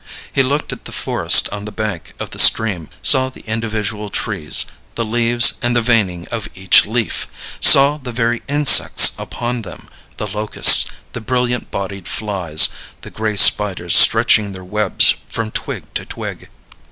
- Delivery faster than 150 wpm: Yes, average, 160 wpm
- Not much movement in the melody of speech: No, average, 3.1 semitones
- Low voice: Yes, low, 110 Hz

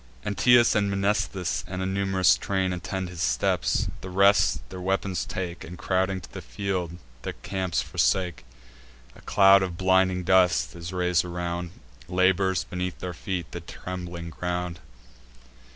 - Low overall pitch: Yes, very low, 90 Hz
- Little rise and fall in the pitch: Yes, narrow, 1.5 semitones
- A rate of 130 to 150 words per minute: Yes, average, 145 wpm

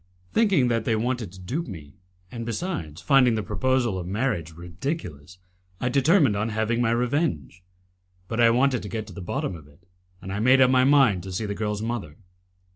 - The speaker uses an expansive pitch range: Yes, wide, 5.7 semitones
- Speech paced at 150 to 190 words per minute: No, average, 200 wpm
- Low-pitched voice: Yes, low, 115 Hz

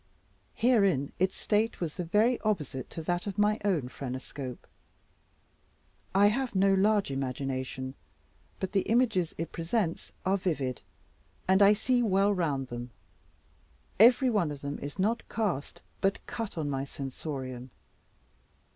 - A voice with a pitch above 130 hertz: Yes, medium, 185 Hz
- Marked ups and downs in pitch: Yes, wide, 7.1 semitones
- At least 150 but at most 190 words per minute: No, average, 140 wpm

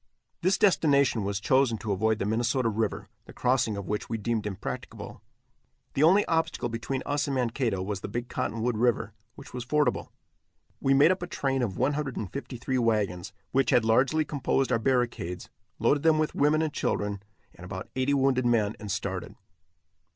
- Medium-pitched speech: No, low, 125 Hz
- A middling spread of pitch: Yes, average, 4.3 semitones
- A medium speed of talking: Yes, average, 175 wpm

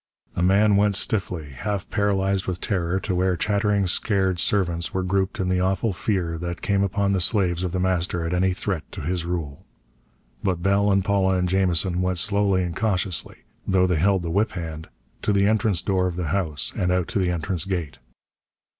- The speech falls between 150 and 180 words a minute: No, average, 200 wpm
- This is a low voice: Yes, very low, 95 Hz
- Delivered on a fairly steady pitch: Yes, narrow, 2.2 semitones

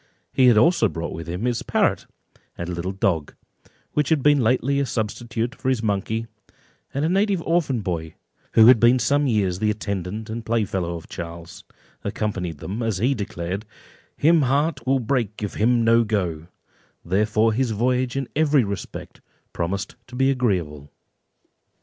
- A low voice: Yes, low, 110 Hz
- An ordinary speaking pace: Yes, average, 165 wpm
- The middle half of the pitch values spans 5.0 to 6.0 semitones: Yes, average, 5.3 semitones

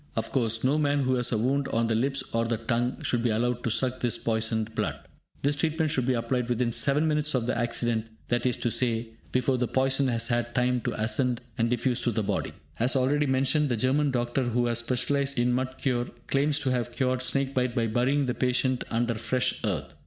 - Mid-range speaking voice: No, low, 125 Hz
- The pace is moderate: No, fast, 225 wpm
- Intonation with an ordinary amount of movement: No, narrow, 2.1 semitones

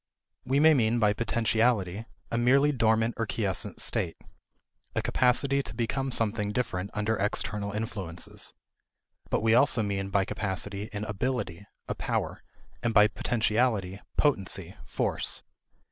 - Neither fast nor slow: No, slow, 130 wpm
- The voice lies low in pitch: Yes, low, 110 Hz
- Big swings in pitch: No, average, 3.2 semitones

